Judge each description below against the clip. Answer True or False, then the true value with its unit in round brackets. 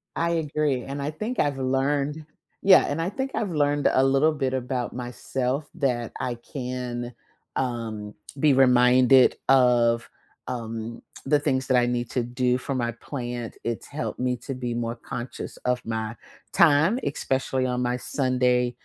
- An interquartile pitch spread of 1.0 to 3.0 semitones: True (2.7 semitones)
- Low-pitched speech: True (130 Hz)